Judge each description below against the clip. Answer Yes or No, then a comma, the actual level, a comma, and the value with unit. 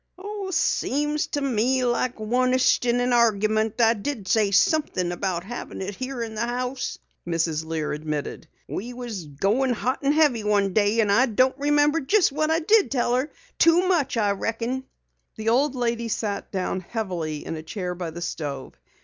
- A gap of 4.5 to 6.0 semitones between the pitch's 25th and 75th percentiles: Yes, average, 5.0 semitones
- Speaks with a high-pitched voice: Yes, high, 230 Hz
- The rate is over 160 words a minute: Yes, average, 180 wpm